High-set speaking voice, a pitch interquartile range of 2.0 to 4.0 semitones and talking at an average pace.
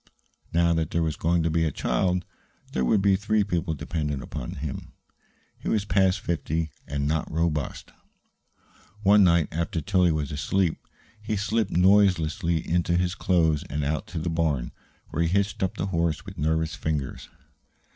No: very low, 85 Hz; average, 3.3 semitones; average, 165 wpm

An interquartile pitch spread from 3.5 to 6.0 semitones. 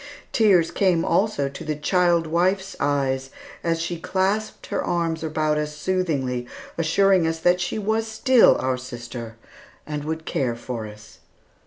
Yes: average, 5.1 semitones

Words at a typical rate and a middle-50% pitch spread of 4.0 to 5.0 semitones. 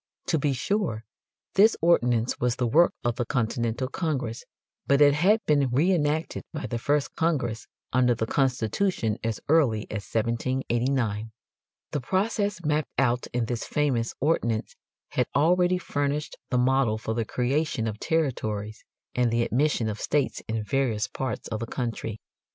Yes: average, 155 wpm; average, 4.7 semitones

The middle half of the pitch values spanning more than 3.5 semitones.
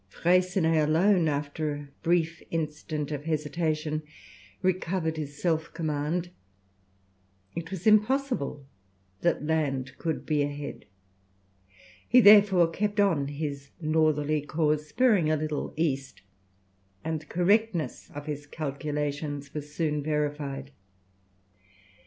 No: narrow, 2.6 semitones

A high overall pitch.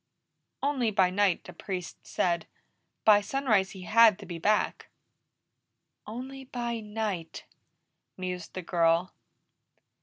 Yes: high, 200 Hz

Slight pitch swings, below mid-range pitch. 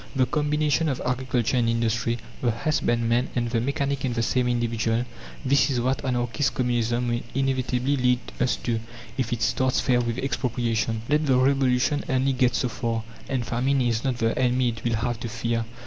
Yes: narrow, 2.0 semitones; low, 125 Hz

